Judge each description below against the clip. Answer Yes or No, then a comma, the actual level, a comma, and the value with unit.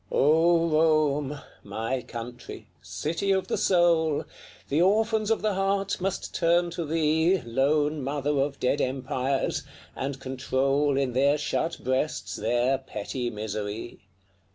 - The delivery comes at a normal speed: No, slow, 130 wpm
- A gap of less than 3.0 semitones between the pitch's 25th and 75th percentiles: No, average, 4.2 semitones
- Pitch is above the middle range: No, medium, 145 Hz